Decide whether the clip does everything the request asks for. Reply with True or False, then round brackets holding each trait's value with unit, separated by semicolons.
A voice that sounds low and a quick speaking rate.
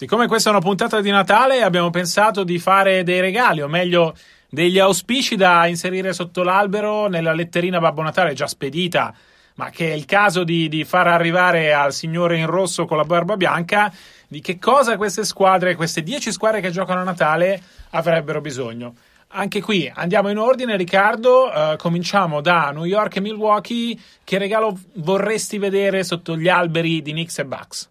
False (185 Hz; 175 wpm)